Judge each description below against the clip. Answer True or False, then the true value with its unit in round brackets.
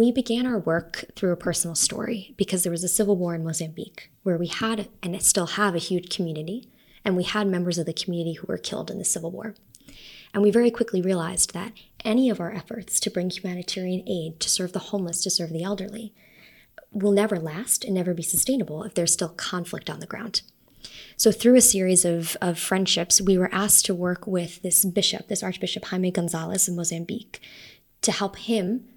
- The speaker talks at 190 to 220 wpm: True (205 wpm)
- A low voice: False (190 Hz)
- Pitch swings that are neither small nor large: True (3.3 semitones)